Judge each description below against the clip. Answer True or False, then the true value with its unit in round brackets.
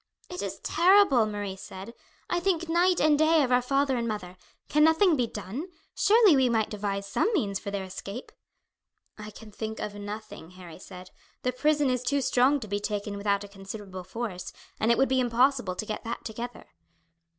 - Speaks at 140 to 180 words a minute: False (195 wpm)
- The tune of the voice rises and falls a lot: True (5.8 semitones)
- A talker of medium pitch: False (230 Hz)